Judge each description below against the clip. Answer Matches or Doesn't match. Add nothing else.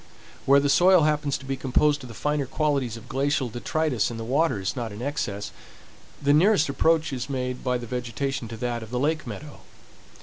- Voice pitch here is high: Doesn't match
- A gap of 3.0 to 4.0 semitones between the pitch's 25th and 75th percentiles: Matches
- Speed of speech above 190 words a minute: Matches